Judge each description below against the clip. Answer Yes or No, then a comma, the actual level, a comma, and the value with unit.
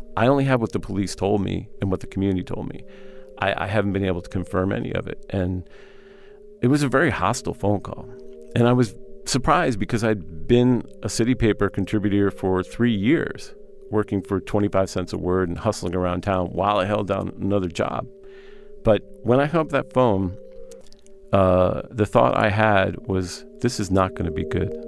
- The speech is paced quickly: No, average, 195 wpm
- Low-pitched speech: Yes, low, 100 Hz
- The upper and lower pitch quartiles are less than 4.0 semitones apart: No, average, 4.8 semitones